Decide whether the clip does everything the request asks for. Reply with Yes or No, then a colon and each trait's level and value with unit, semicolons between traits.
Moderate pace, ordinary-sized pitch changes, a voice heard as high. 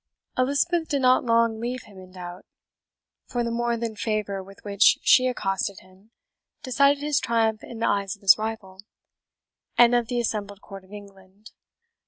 Yes: average, 170 wpm; average, 3.5 semitones; high, 220 Hz